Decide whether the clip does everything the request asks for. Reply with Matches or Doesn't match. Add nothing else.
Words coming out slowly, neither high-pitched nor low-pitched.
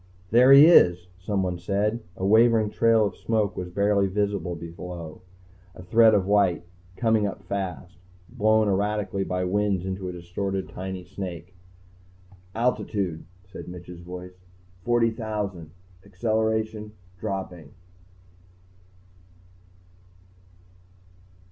Doesn't match